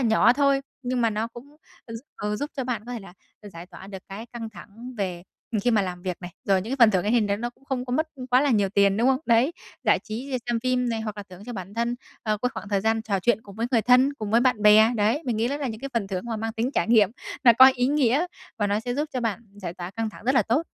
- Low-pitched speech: No, high, 225 Hz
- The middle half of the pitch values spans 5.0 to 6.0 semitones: No, average, 3.3 semitones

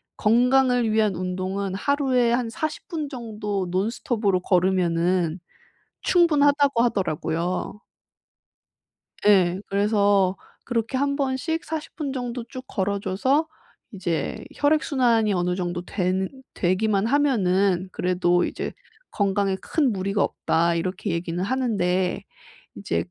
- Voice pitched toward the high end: Yes, high, 205 Hz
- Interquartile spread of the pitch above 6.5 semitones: No, wide, 5.5 semitones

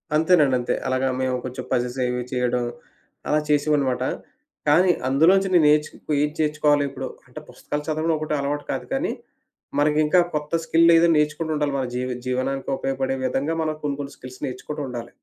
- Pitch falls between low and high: Yes, medium, 145 Hz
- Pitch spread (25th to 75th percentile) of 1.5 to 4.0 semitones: Yes, average, 2.9 semitones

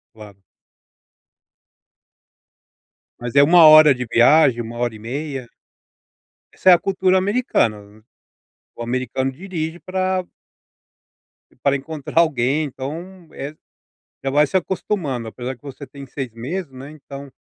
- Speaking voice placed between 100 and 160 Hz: Yes, medium, 140 Hz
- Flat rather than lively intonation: No, average, 5.1 semitones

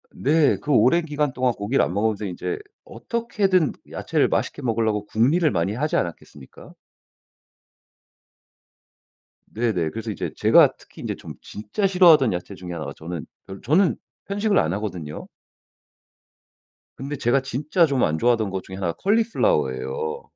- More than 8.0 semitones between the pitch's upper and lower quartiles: Yes, wide, 8.7 semitones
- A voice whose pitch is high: No, low, 120 Hz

